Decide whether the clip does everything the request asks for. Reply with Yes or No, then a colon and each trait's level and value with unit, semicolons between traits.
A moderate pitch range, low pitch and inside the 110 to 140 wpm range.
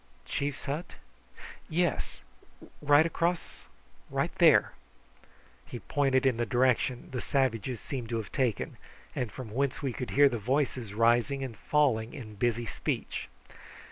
Yes: average, 3.3 semitones; low, 130 Hz; slow, 135 wpm